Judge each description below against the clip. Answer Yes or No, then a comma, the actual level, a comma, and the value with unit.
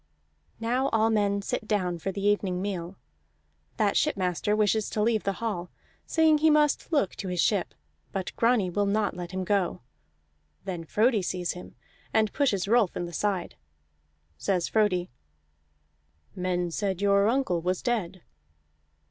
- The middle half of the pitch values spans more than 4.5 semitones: No, average, 3.4 semitones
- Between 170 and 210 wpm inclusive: No, average, 150 wpm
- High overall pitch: Yes, high, 200 Hz